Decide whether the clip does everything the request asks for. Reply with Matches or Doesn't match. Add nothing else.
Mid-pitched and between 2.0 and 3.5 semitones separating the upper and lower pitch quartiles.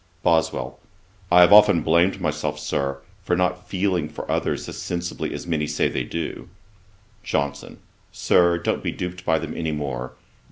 Doesn't match